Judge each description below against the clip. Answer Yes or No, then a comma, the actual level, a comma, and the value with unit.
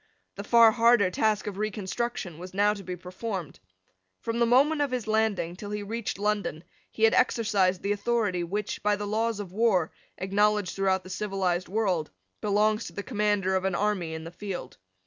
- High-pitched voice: Yes, high, 205 Hz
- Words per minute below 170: No, average, 185 wpm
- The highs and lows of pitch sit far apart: No, average, 2.8 semitones